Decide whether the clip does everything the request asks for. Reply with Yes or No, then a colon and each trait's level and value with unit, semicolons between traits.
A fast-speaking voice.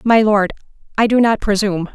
No: average, 185 wpm